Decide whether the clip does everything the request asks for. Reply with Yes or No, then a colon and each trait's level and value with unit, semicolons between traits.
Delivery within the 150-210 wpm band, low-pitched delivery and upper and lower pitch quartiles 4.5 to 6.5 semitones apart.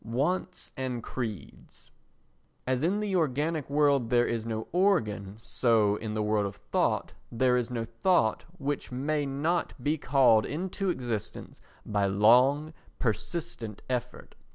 No: slow, 135 wpm; low, 125 Hz; wide, 5.5 semitones